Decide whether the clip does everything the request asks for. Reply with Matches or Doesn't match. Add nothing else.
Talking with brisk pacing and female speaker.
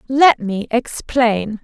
Doesn't match